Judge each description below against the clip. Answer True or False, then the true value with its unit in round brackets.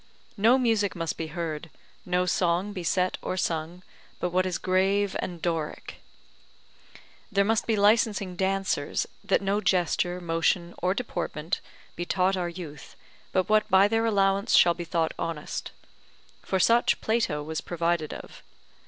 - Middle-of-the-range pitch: True (180 Hz)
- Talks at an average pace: True (150 wpm)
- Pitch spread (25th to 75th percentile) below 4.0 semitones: True (2.8 semitones)